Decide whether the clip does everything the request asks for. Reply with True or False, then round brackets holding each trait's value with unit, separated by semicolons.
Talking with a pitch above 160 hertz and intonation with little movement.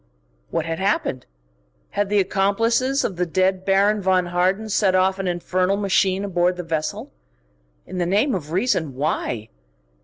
True (185 Hz; 2.2 semitones)